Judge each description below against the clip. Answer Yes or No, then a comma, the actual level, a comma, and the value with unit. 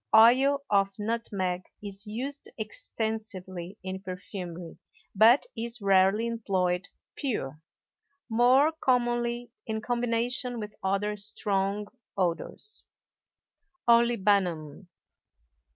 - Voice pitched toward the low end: No, high, 210 Hz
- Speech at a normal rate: No, slow, 85 wpm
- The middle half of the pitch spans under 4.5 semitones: Yes, average, 3.8 semitones